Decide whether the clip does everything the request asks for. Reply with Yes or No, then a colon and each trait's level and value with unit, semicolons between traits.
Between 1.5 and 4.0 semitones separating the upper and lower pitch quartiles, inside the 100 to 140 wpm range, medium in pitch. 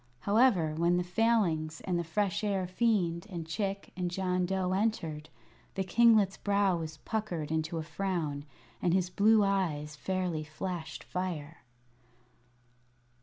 Yes: average, 3.5 semitones; slow, 135 wpm; medium, 180 Hz